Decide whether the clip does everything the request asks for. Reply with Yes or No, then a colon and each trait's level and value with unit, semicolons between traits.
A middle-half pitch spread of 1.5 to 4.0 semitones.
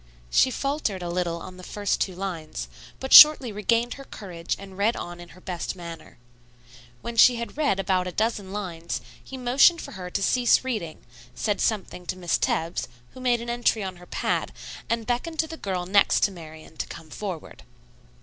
No: average, 5.2 semitones